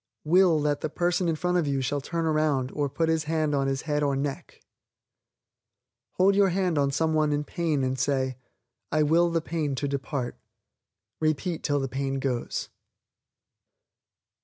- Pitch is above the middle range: No, medium, 150 Hz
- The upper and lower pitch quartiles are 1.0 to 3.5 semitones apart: Yes, average, 3.0 semitones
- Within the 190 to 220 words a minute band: No, average, 170 wpm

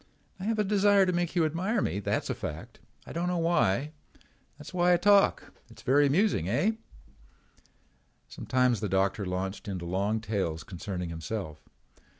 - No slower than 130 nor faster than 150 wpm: No, average, 160 wpm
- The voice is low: Yes, low, 125 Hz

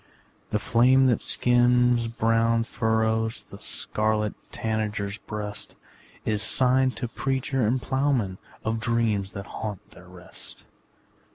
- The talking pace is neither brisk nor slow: No, slow, 115 wpm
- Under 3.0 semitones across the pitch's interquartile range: Yes, narrow, 2.4 semitones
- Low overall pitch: Yes, low, 115 Hz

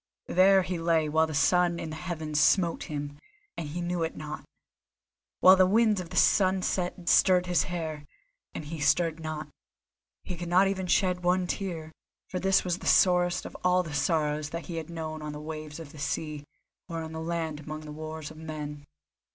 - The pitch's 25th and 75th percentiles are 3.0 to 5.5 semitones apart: No, narrow, 2.6 semitones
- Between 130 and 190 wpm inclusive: No, average, 200 wpm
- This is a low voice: No, medium, 165 Hz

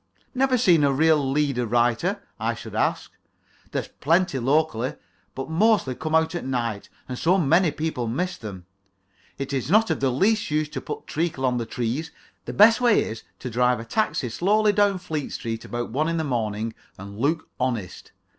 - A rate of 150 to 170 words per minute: No, average, 185 wpm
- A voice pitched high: No, medium, 140 Hz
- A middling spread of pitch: No, wide, 6.1 semitones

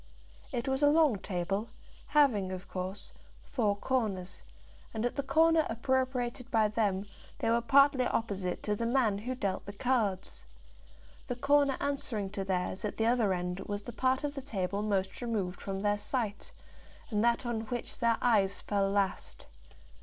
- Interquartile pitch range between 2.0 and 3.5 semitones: No, average, 4.6 semitones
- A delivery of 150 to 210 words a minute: Yes, average, 170 wpm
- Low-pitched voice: No, high, 220 Hz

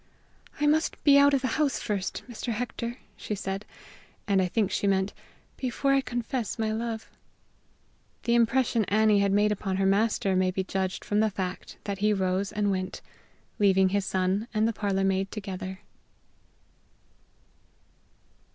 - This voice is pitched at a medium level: No, high, 205 Hz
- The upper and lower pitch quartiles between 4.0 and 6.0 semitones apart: No, average, 3.2 semitones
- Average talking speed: Yes, average, 160 wpm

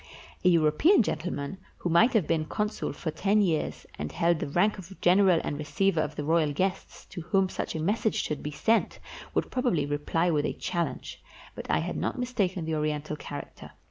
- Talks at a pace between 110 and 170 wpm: No, average, 195 wpm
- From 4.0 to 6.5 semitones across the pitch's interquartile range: Yes, average, 4.3 semitones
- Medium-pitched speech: Yes, medium, 170 Hz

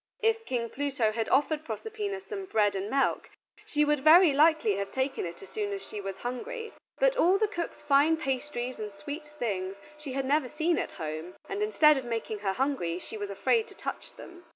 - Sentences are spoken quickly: Yes, fast, 210 wpm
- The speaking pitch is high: Yes, very high, 275 Hz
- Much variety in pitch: Yes, wide, 8.2 semitones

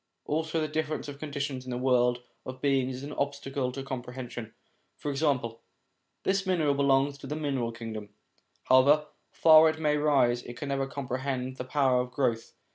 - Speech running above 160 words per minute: Yes, average, 175 wpm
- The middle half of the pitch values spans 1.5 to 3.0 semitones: Yes, average, 2.7 semitones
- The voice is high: No, low, 135 Hz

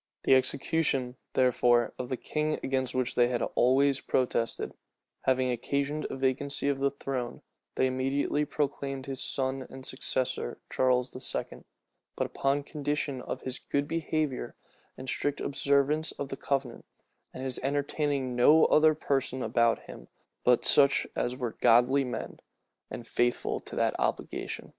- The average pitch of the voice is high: No, low, 135 Hz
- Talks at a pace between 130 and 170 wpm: Yes, average, 145 wpm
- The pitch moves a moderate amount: No, narrow, 2.0 semitones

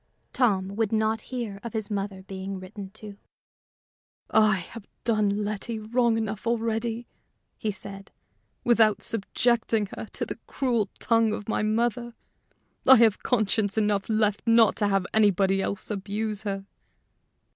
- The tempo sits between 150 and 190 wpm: No, average, 140 wpm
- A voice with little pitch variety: Yes, narrow, 2.3 semitones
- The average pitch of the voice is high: Yes, high, 215 Hz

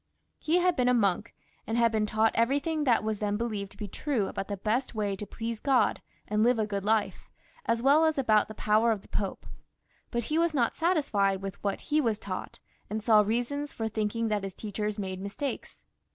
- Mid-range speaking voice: No, high, 220 Hz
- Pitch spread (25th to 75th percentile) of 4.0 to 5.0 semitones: No, average, 3.4 semitones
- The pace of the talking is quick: Yes, fast, 215 wpm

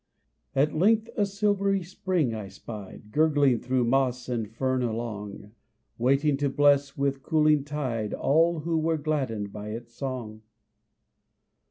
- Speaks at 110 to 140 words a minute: Yes, slow, 135 wpm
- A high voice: No, low, 135 Hz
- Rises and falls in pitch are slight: No, average, 5.0 semitones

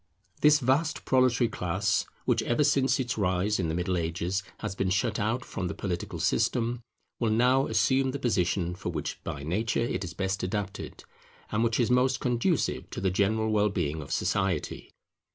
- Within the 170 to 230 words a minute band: Yes, average, 180 wpm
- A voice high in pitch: No, low, 105 Hz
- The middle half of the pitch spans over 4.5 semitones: Yes, average, 4.9 semitones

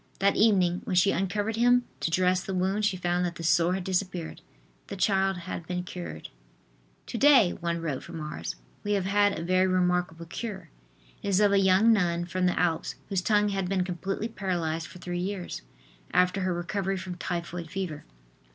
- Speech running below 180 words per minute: No, average, 190 wpm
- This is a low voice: No, medium, 185 Hz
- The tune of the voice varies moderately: No, narrow, 2.1 semitones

